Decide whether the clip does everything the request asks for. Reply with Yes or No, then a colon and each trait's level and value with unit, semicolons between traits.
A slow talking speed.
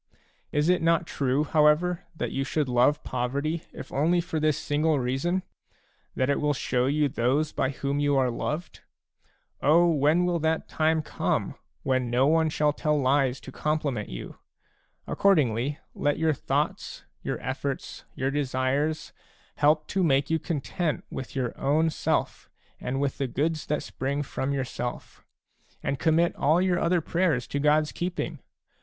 No: average, 160 wpm